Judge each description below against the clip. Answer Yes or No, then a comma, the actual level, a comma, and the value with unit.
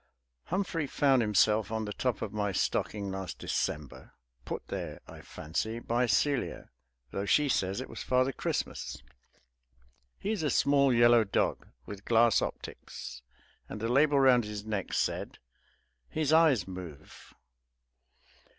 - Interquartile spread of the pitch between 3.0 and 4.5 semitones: No, average, 5.0 semitones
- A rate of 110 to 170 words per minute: Yes, average, 140 wpm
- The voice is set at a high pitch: No, low, 115 Hz